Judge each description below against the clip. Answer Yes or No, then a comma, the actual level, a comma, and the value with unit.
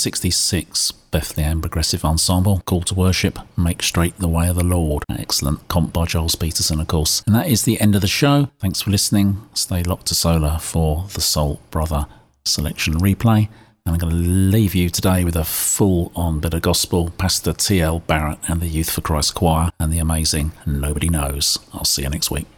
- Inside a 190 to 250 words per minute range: Yes, average, 200 wpm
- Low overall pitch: Yes, very low, 85 Hz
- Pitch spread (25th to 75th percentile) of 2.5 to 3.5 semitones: Yes, average, 3.2 semitones